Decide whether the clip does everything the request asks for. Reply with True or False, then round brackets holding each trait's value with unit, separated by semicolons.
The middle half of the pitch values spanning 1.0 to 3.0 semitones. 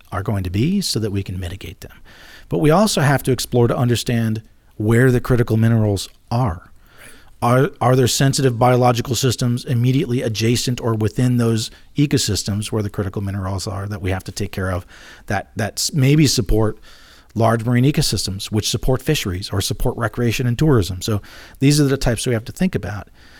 False (3.8 semitones)